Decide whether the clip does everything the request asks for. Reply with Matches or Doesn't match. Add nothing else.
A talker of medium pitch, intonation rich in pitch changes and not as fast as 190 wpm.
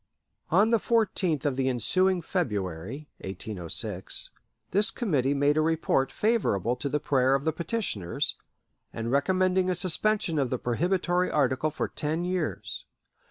Matches